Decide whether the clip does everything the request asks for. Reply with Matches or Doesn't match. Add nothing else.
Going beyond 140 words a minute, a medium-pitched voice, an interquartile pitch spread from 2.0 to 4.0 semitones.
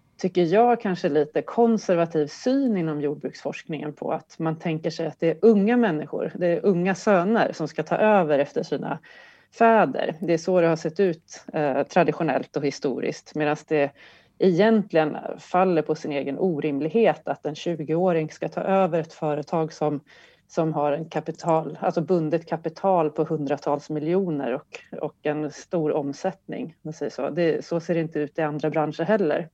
Matches